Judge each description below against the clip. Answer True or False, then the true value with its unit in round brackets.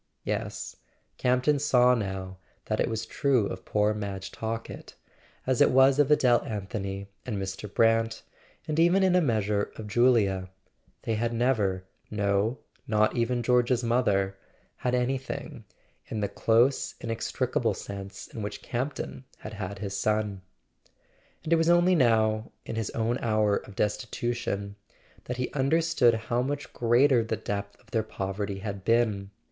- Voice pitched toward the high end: False (115 Hz)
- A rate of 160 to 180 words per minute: False (150 wpm)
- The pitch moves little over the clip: False (3.7 semitones)